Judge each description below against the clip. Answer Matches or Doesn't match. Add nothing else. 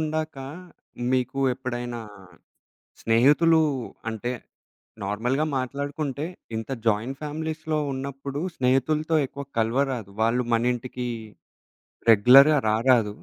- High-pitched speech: Doesn't match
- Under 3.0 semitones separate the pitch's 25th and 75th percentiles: Doesn't match